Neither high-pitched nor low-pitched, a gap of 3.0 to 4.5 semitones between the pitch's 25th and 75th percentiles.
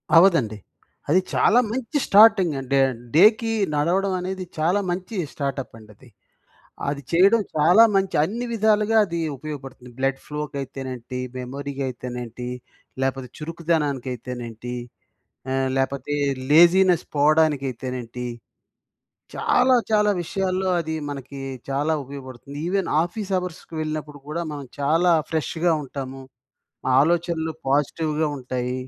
No: medium, 150 Hz; wide, 5.4 semitones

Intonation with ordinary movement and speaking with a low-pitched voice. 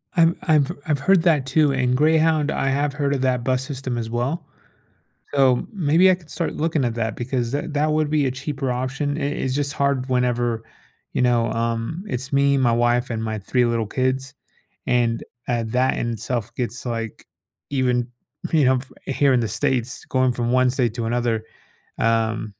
Yes: average, 3.2 semitones; low, 130 Hz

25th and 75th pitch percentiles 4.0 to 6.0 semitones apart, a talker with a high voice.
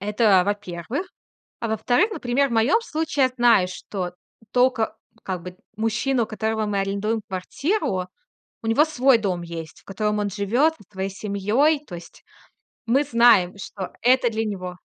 Yes: average, 4.4 semitones; high, 220 Hz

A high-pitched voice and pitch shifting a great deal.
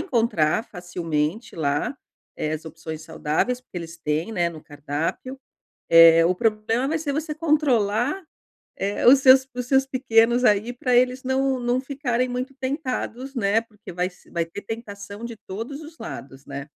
Yes: high, 225 Hz; wide, 7.4 semitones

